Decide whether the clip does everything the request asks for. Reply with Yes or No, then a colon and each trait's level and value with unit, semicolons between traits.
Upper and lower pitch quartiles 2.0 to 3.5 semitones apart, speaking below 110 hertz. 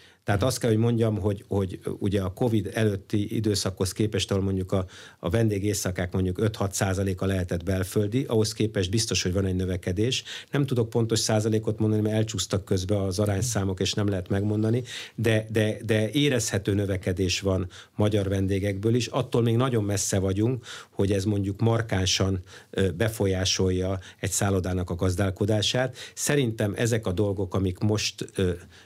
Yes: narrow, 2.5 semitones; low, 100 Hz